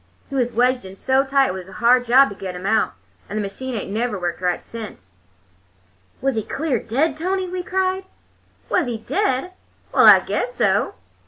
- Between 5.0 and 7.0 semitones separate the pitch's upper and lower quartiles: Yes, wide, 5.6 semitones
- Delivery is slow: No, average, 195 wpm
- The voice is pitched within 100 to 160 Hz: No, high, 245 Hz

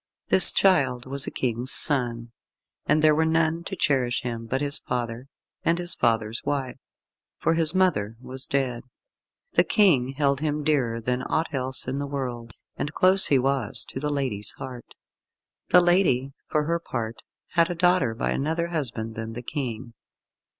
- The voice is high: No, low, 135 Hz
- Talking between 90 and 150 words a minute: No, average, 170 wpm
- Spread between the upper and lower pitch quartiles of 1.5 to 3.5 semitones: No, average, 4.6 semitones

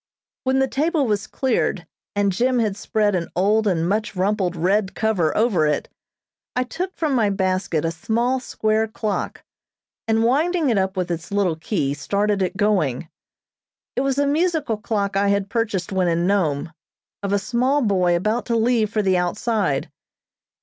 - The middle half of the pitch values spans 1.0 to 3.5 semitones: No, average, 4.2 semitones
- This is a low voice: No, high, 205 Hz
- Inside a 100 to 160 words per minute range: No, average, 170 wpm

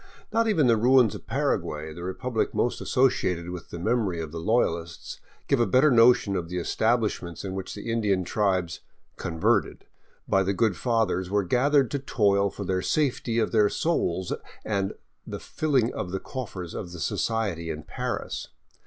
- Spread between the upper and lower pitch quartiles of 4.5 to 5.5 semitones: Yes, average, 5.2 semitones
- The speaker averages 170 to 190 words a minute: Yes, average, 180 wpm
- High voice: No, low, 100 Hz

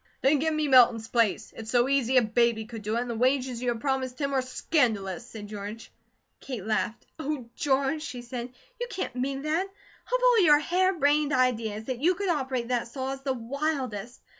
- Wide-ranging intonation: No, average, 4.0 semitones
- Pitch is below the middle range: No, very high, 255 Hz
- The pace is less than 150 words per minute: No, fast, 205 wpm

